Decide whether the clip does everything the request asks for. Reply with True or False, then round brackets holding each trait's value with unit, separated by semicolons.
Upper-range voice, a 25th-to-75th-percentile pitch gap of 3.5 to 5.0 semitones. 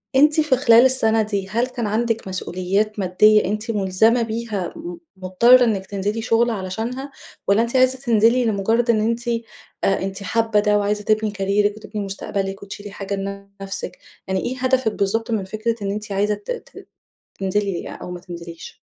False (210 Hz; 2.9 semitones)